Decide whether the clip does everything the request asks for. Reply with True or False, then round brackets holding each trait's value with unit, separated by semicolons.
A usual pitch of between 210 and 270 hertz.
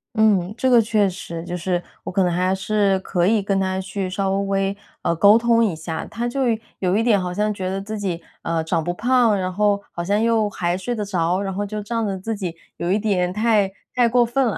False (195 Hz)